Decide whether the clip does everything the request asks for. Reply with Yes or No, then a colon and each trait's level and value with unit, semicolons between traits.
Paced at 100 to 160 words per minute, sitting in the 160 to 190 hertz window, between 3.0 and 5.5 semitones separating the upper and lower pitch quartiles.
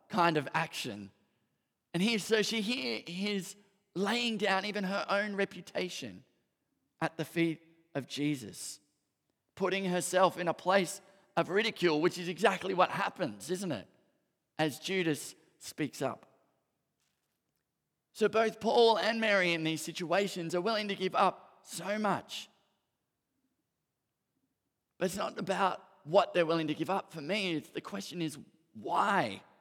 Yes: average, 140 wpm; medium, 185 Hz; average, 3.5 semitones